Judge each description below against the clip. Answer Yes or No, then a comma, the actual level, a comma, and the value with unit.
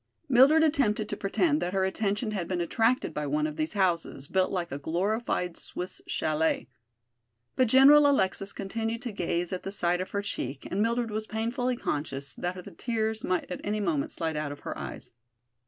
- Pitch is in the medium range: No, high, 195 Hz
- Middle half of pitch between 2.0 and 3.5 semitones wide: No, average, 4.9 semitones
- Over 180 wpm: Yes, average, 190 wpm